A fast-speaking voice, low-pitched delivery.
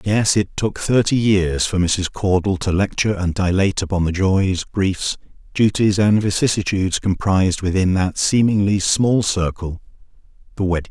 No: average, 150 wpm; very low, 95 Hz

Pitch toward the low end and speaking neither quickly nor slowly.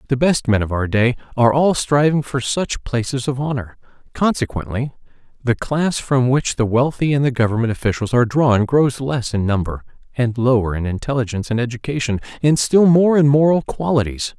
Yes: low, 130 Hz; average, 180 wpm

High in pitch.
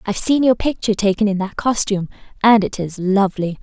Yes: high, 205 Hz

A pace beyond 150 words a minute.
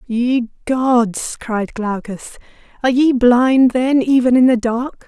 No: average, 140 wpm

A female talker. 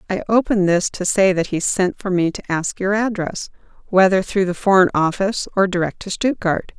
Yes: female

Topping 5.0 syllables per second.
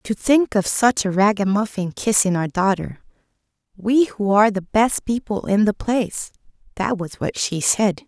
No: 4.6 syllables/s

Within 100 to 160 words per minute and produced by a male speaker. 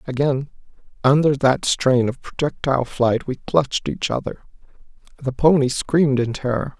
Yes: average, 140 wpm; male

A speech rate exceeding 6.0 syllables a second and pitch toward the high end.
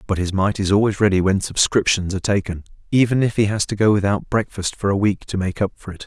No: 6.2 syllables/s; low, 100 Hz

